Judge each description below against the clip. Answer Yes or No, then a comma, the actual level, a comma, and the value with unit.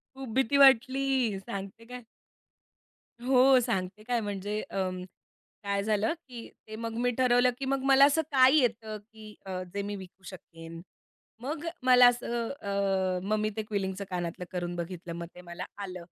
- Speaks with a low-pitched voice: No, high, 215 Hz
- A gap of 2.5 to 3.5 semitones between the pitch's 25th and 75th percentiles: No, average, 4.8 semitones